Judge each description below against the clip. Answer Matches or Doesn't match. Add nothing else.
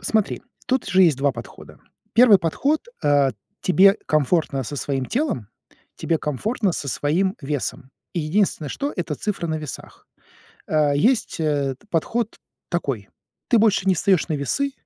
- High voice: Doesn't match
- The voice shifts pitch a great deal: Matches